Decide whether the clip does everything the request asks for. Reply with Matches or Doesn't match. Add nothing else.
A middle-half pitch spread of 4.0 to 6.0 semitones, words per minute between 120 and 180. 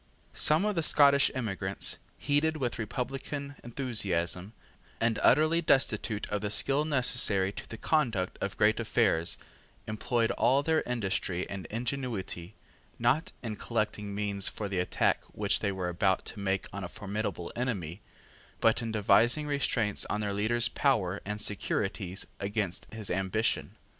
Matches